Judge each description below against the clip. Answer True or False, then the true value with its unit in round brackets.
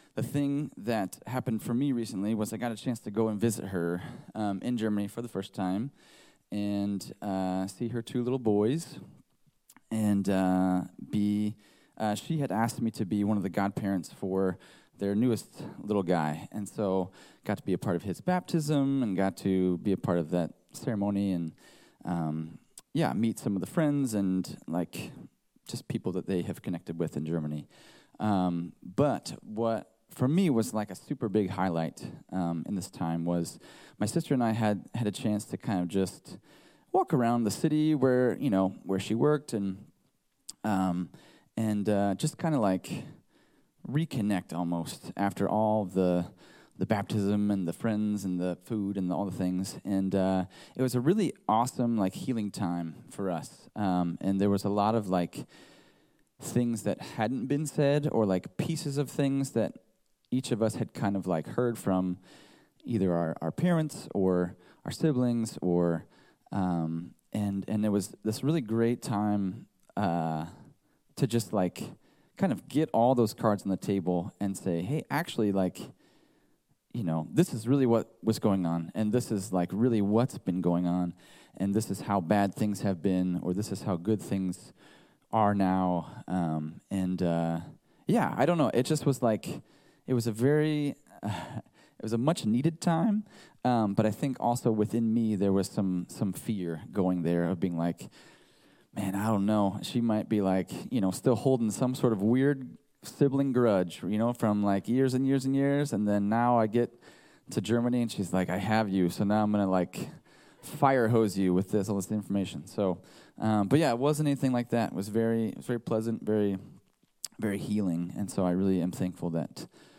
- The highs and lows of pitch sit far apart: False (4.2 semitones)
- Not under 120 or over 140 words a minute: False (190 wpm)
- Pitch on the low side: True (105 Hz)